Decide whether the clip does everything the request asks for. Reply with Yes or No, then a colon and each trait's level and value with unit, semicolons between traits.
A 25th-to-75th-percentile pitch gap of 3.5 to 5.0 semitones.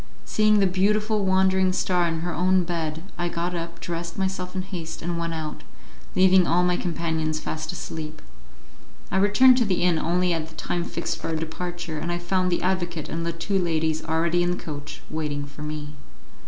No: narrow, 2.4 semitones